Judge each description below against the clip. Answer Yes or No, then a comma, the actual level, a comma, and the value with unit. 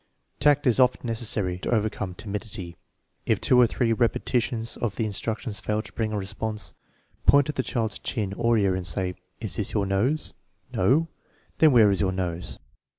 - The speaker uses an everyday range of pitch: Yes, average, 3.6 semitones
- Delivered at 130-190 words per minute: No, fast, 205 wpm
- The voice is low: Yes, low, 110 Hz